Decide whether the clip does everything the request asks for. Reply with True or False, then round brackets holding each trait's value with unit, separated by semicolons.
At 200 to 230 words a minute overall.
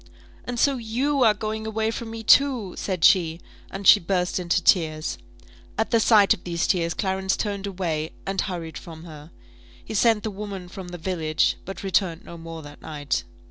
False (185 wpm)